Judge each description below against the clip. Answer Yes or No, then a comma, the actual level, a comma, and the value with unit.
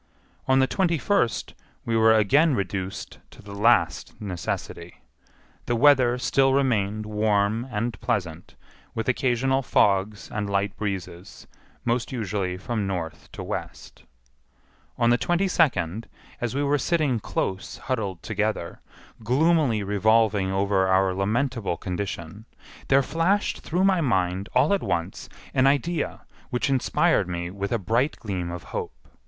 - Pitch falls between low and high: No, low, 110 Hz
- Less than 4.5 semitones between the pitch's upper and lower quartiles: No, average, 5.3 semitones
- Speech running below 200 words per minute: Yes, slow, 135 wpm